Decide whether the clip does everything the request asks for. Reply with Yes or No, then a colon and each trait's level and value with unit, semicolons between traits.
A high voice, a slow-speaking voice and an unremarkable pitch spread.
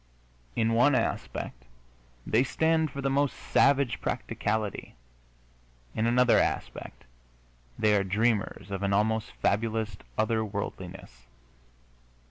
No: low, 110 Hz; slow, 105 wpm; average, 3.7 semitones